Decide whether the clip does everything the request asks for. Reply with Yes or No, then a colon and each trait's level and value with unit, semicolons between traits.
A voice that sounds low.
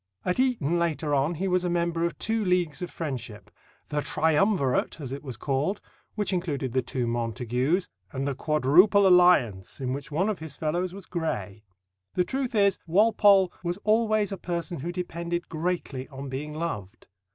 No: medium, 170 Hz